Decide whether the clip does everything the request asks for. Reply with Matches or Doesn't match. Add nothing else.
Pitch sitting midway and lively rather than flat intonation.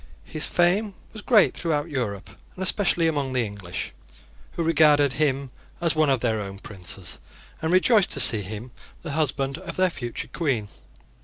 Matches